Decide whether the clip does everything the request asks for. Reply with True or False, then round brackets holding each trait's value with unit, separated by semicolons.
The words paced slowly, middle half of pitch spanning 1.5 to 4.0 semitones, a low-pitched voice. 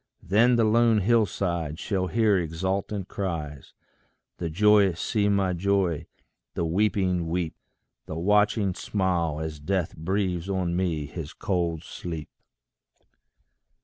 True (120 wpm; 3.5 semitones; 90 Hz)